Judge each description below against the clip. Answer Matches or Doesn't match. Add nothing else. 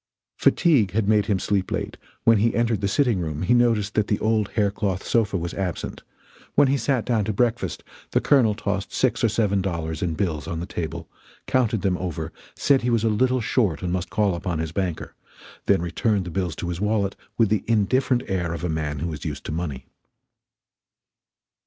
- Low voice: Matches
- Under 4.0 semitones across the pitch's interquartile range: Doesn't match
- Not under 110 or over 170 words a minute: Doesn't match